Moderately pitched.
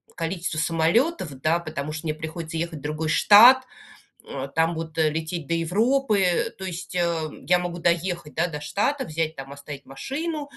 Yes: medium, 165 Hz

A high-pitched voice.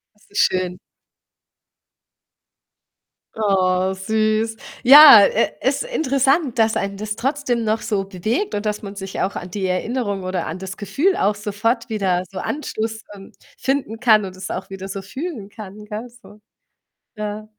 Yes: high, 210 Hz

